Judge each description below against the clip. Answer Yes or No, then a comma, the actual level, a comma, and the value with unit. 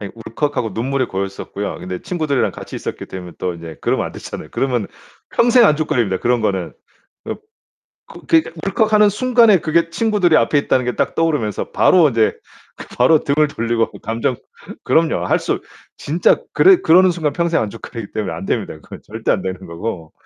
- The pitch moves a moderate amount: No, wide, 8.2 semitones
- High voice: No, low, 130 Hz